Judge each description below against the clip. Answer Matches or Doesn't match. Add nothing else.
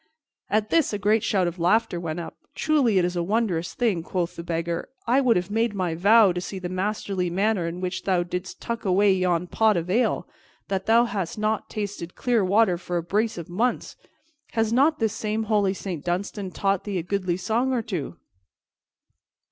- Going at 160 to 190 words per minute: Doesn't match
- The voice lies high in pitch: Matches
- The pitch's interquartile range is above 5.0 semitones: Doesn't match